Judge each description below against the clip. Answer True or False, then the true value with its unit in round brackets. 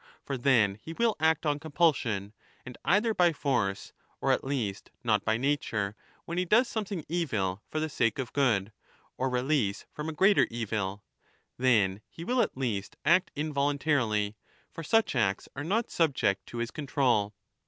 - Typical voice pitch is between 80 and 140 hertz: True (135 Hz)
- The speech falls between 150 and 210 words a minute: True (175 wpm)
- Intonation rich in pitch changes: True (6.9 semitones)